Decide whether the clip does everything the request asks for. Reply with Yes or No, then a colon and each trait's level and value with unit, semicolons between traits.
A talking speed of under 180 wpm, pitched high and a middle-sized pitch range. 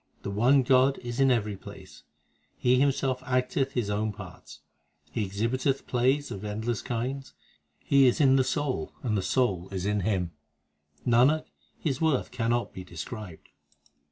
No: average, 155 wpm; low, 120 Hz; average, 4.2 semitones